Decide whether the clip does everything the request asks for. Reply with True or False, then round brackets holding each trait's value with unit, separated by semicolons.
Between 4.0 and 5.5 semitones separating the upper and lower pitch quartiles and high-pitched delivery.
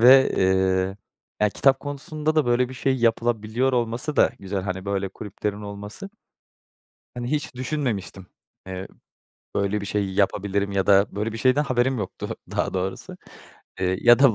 False (4.8 semitones; 105 Hz)